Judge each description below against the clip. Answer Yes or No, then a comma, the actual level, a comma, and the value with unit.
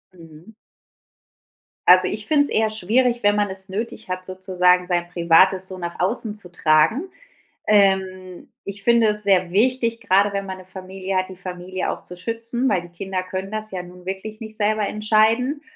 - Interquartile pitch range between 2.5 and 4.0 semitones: Yes, average, 2.9 semitones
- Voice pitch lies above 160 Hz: Yes, high, 190 Hz